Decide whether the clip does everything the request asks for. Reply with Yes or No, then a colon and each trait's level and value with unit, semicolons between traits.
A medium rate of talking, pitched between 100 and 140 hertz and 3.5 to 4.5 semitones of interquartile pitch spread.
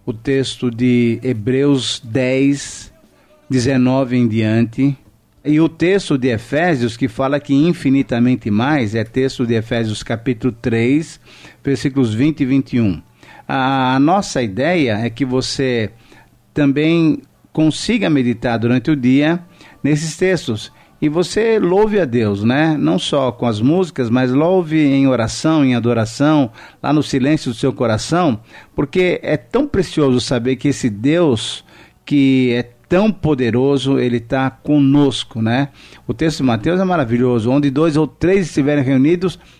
Yes: average, 140 wpm; low, 135 Hz; average, 3.8 semitones